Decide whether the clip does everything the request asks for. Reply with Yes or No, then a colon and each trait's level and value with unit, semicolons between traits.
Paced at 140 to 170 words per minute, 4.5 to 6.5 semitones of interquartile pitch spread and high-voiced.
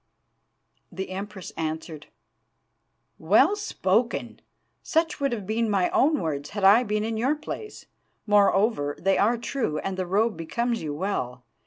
Yes: average, 145 wpm; average, 4.9 semitones; high, 205 Hz